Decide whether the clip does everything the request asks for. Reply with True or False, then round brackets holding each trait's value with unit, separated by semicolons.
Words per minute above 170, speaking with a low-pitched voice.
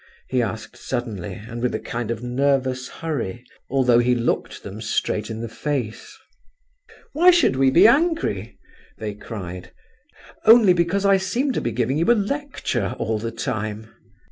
False (160 wpm; 125 Hz)